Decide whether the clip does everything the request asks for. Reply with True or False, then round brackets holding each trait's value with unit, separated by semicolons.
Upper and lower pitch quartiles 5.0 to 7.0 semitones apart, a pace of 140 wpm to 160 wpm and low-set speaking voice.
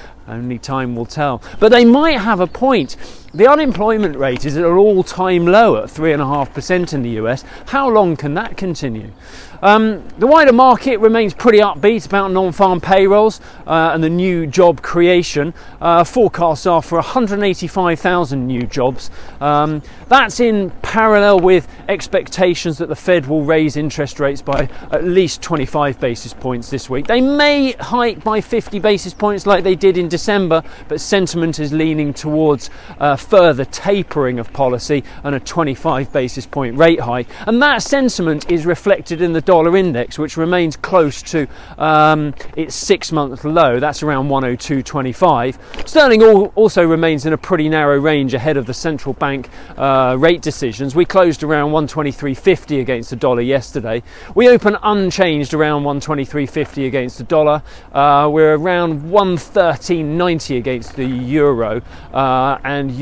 False (5.3 semitones; 155 wpm; 160 Hz)